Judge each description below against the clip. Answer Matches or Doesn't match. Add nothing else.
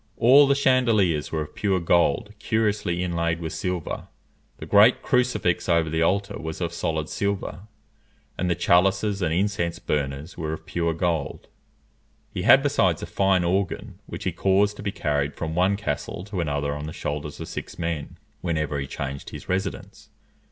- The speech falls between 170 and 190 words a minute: Matches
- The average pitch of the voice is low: Matches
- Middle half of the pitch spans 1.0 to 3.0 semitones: Doesn't match